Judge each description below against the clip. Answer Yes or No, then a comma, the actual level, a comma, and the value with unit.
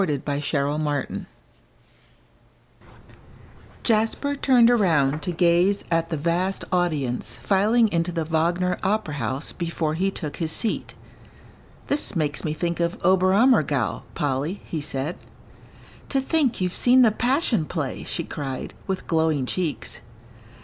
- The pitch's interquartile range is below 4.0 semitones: No, average, 4.8 semitones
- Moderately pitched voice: Yes, medium, 170 Hz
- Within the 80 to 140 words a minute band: Yes, slow, 135 wpm